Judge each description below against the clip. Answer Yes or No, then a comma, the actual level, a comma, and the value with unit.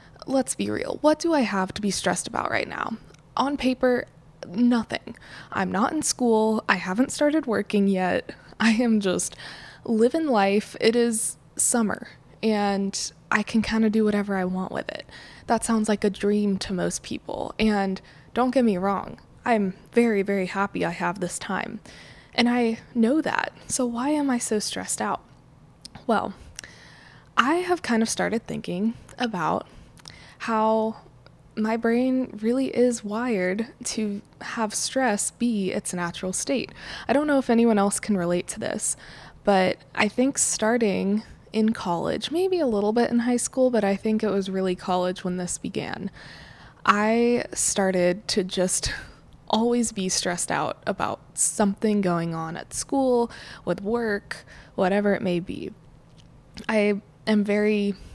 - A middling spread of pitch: Yes, average, 3.6 semitones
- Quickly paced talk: No, average, 160 wpm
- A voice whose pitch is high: Yes, high, 215 Hz